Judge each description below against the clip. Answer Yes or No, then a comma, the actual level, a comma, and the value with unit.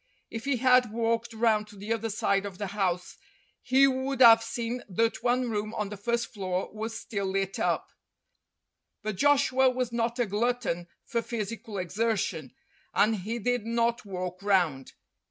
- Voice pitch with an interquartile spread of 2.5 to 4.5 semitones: Yes, average, 3.1 semitones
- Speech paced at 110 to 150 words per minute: No, average, 165 wpm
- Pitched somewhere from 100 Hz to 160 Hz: No, high, 225 Hz